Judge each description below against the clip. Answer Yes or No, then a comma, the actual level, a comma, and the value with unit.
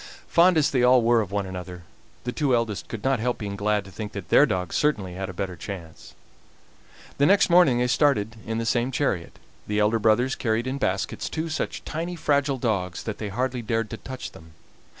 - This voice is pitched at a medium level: No, low, 115 Hz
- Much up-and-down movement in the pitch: No, average, 4.9 semitones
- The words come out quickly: Yes, fast, 210 wpm